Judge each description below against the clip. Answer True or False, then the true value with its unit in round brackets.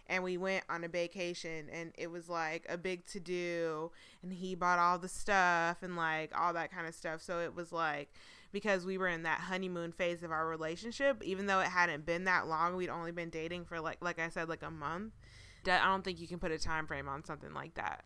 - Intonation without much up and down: True (2.0 semitones)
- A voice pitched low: False (175 Hz)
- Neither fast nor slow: False (245 wpm)